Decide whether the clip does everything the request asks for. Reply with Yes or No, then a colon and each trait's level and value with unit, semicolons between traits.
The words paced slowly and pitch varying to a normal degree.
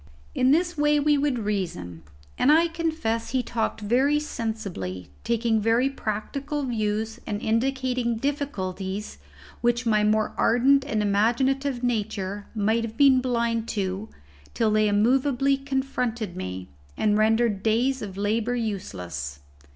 Yes: slow, 130 wpm; average, 4.3 semitones